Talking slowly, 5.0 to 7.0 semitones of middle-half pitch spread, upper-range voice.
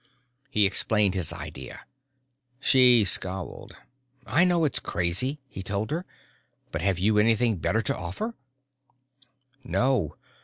No: slow, 125 wpm; wide, 5.4 semitones; low, 110 Hz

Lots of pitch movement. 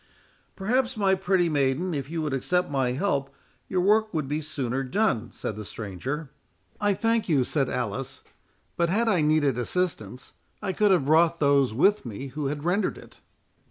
Yes: wide, 5.9 semitones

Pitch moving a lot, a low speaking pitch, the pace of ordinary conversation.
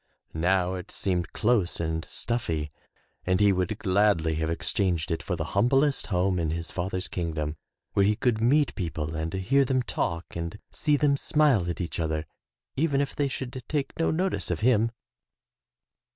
Yes: wide, 7.0 semitones; very low, 95 Hz; average, 175 wpm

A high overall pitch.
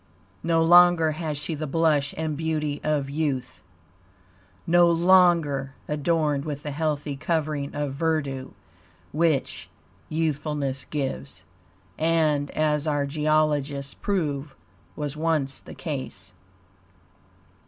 No: medium, 150 Hz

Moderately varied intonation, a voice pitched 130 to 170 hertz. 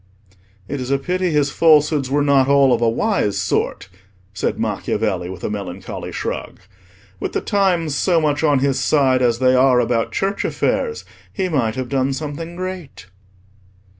Yes: average, 4.5 semitones; medium, 140 Hz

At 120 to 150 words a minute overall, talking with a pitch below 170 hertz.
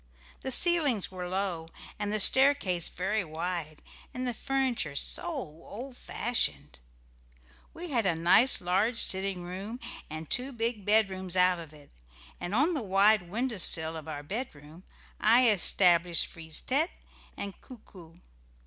No: average, 145 wpm; high, 195 Hz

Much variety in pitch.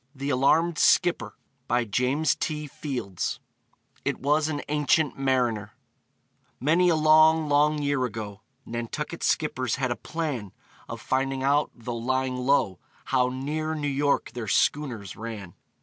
No: average, 3.9 semitones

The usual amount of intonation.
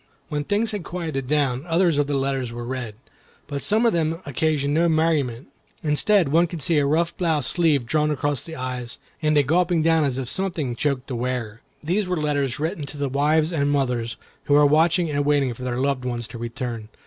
Yes: average, 4.1 semitones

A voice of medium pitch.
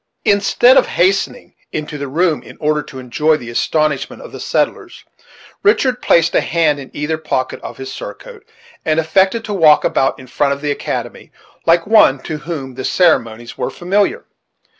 Yes: medium, 155 Hz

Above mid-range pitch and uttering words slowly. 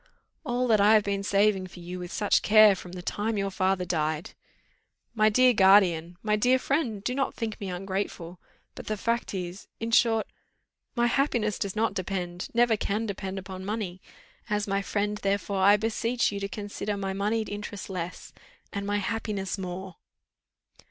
No: high, 200 Hz; average, 175 wpm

